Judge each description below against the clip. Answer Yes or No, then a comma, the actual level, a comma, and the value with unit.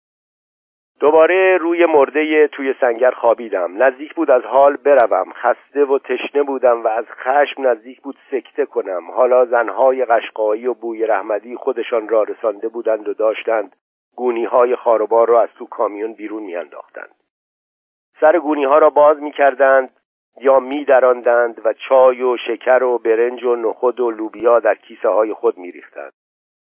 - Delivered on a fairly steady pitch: No, average, 4.2 semitones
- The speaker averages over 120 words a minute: Yes, fast, 155 wpm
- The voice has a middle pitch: No, low, 130 Hz